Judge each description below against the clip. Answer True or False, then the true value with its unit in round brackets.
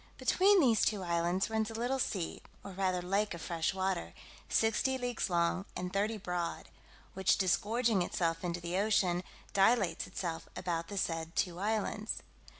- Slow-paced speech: False (155 wpm)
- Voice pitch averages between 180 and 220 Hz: True (190 Hz)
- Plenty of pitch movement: False (3.9 semitones)